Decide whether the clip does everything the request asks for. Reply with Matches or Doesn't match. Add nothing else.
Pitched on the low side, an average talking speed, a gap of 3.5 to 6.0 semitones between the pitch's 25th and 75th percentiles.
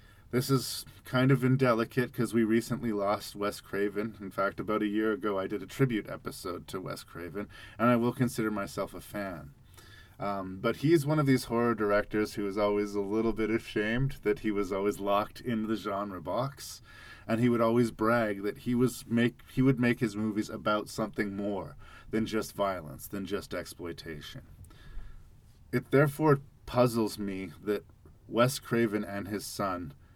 Doesn't match